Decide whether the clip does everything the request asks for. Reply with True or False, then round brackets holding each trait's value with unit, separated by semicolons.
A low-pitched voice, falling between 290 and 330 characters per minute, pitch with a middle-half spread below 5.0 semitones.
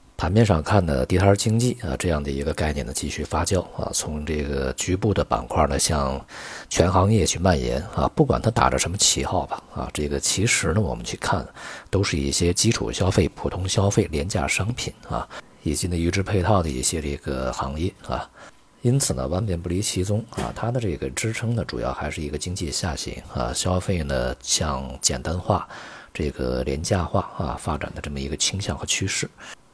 False (85 Hz; 295 characters per minute; 5.6 semitones)